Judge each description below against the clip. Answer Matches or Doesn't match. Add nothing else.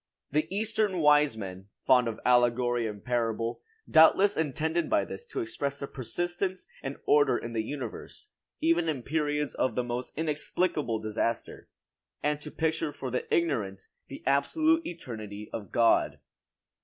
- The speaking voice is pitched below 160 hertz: Matches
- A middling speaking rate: Matches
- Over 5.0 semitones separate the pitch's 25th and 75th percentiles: Matches